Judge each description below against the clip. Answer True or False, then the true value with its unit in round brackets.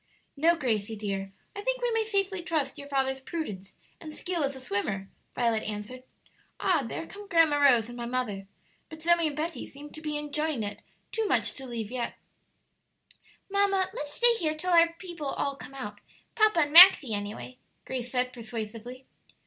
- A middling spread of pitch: False (6.2 semitones)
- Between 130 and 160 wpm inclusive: False (180 wpm)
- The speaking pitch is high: True (280 Hz)